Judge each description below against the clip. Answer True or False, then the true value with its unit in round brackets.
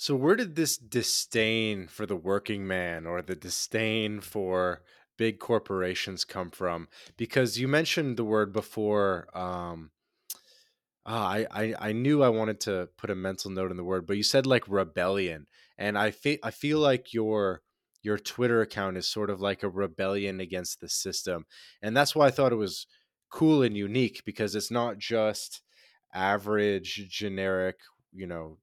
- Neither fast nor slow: True (170 wpm)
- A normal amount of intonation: True (3.3 semitones)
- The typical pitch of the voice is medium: False (105 Hz)